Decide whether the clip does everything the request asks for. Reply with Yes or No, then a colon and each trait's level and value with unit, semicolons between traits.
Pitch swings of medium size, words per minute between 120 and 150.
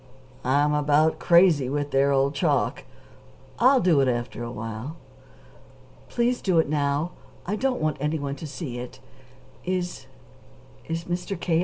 Yes: average, 4.1 semitones; average, 145 wpm